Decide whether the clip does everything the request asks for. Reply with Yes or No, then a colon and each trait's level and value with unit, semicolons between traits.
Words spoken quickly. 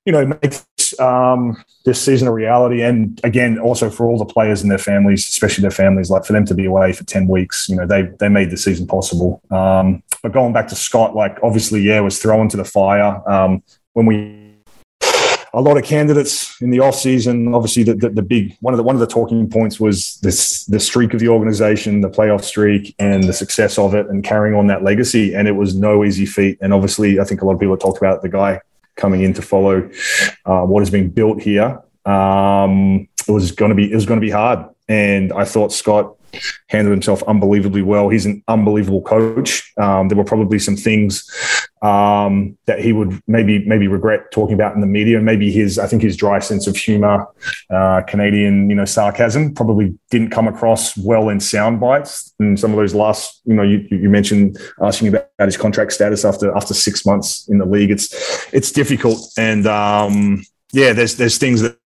Yes: fast, 215 wpm